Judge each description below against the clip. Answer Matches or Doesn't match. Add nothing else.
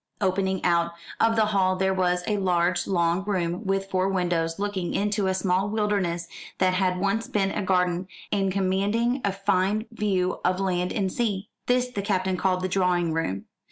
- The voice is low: Doesn't match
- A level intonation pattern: Matches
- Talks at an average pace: Matches